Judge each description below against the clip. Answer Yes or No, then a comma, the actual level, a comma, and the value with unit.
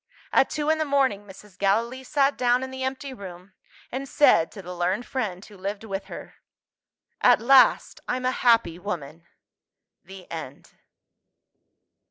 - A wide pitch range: Yes, wide, 5.9 semitones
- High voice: Yes, high, 215 Hz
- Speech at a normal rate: Yes, average, 155 wpm